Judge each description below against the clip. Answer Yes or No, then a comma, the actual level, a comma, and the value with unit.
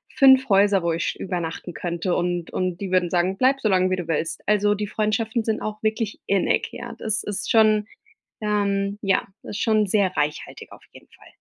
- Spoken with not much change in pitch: No, average, 3.0 semitones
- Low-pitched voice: No, high, 200 Hz